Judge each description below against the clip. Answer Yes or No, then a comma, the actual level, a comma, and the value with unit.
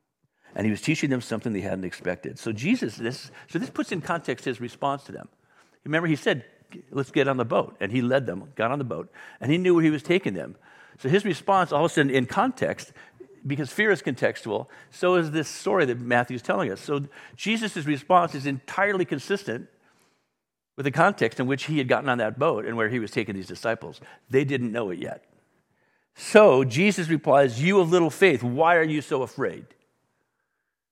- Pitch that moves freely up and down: Yes, wide, 6.0 semitones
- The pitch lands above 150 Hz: No, medium, 145 Hz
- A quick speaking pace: Yes, fast, 210 wpm